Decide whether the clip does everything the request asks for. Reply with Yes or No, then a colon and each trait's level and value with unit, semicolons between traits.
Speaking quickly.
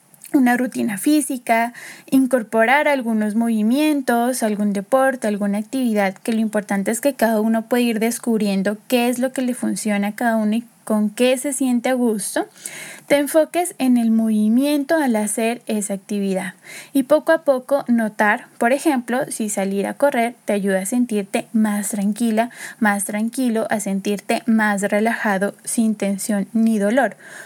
No: average, 155 wpm